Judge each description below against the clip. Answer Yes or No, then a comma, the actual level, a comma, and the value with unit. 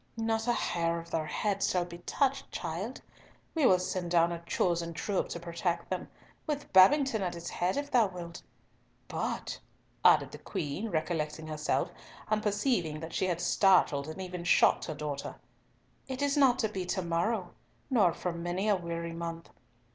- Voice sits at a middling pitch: Yes, medium, 180 Hz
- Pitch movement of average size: Yes, average, 4.1 semitones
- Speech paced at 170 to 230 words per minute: Yes, average, 175 wpm